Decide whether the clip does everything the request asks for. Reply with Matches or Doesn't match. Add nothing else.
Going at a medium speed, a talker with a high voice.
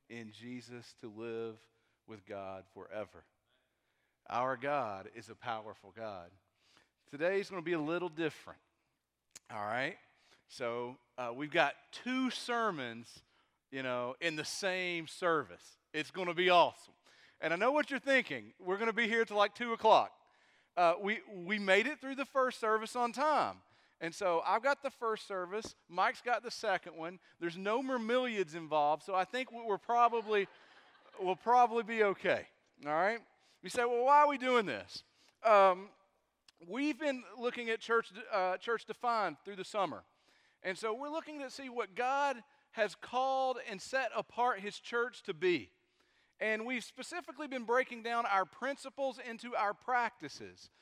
Matches